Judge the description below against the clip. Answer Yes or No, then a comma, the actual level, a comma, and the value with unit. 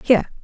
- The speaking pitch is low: No, high, 230 Hz